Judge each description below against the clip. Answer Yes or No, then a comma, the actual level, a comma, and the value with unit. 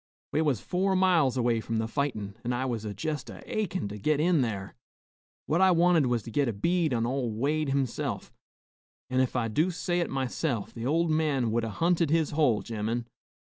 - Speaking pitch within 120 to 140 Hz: Yes, low, 135 Hz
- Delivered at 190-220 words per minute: Yes, fast, 205 wpm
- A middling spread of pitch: No, wide, 5.7 semitones